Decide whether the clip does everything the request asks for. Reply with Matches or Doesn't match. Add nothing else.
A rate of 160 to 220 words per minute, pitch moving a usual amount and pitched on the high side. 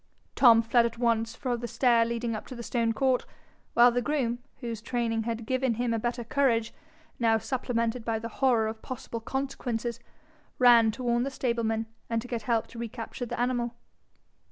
Doesn't match